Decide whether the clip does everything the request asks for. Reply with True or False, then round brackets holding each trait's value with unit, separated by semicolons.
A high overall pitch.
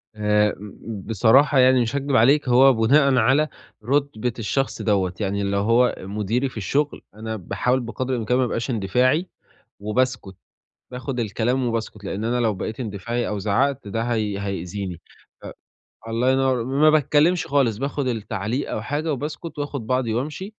False (120 Hz)